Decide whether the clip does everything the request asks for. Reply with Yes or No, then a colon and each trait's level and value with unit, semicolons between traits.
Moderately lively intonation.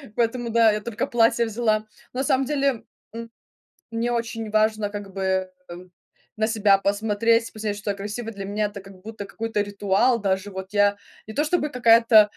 No: narrow, 2.2 semitones